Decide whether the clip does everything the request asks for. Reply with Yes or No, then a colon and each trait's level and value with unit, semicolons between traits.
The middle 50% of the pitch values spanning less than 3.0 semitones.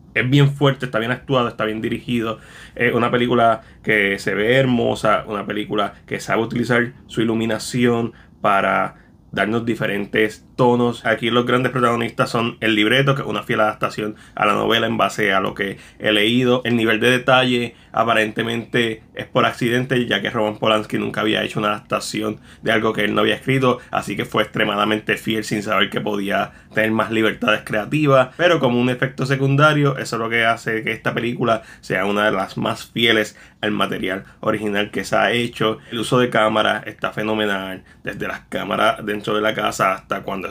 Yes: narrow, 2.4 semitones